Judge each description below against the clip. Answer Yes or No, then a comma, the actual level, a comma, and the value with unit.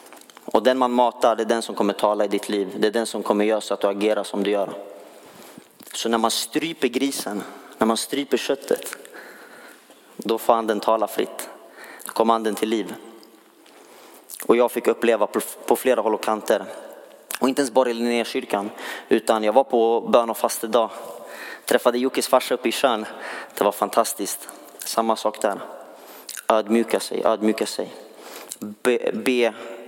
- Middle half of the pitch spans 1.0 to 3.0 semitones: Yes, average, 2.7 semitones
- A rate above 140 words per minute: Yes, average, 175 wpm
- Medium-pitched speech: No, low, 115 Hz